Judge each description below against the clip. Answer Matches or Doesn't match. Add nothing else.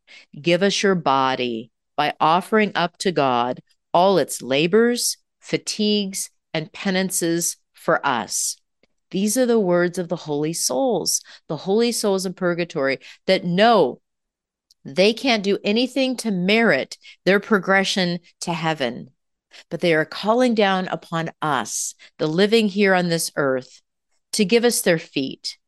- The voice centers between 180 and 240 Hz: Matches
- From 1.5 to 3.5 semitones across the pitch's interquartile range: Doesn't match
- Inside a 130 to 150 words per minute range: Matches